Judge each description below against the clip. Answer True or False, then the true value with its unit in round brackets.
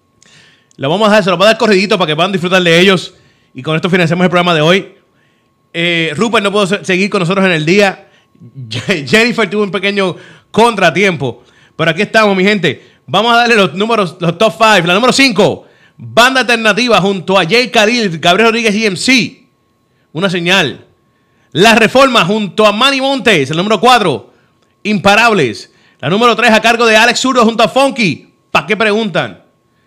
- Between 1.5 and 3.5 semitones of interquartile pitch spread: False (4.4 semitones)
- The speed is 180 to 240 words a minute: True (185 wpm)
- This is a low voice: False (200 Hz)